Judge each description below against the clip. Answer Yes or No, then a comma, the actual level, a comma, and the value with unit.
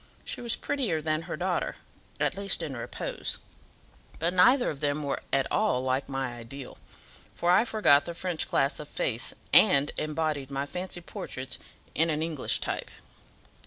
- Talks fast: No, average, 160 wpm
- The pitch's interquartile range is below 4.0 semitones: No, average, 4.4 semitones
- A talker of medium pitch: Yes, medium, 155 Hz